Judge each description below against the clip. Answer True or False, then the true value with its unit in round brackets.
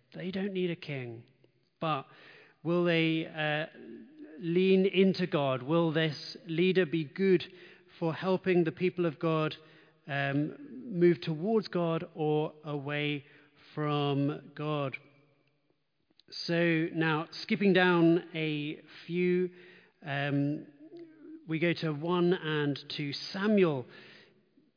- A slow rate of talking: True (110 wpm)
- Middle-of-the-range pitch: True (160 Hz)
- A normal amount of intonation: True (3.4 semitones)